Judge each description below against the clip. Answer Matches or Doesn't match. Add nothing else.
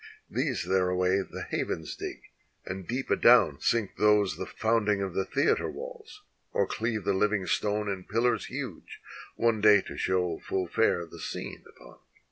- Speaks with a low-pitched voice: Matches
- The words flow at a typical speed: Matches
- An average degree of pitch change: Matches